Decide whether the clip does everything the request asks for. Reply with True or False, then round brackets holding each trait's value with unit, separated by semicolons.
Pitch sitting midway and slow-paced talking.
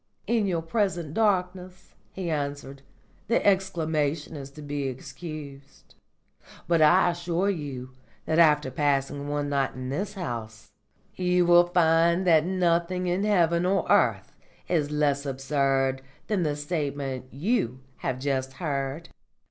True (155 Hz; 130 wpm)